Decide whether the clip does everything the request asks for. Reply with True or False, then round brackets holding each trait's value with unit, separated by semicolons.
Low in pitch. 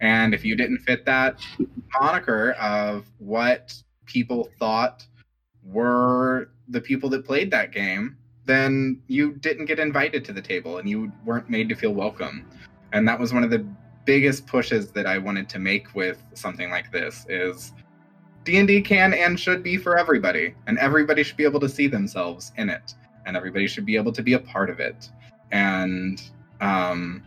True (125 Hz)